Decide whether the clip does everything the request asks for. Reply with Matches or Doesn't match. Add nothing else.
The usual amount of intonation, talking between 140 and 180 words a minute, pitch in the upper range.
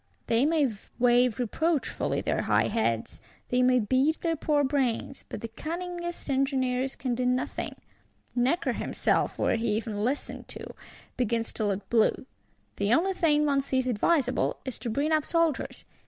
Matches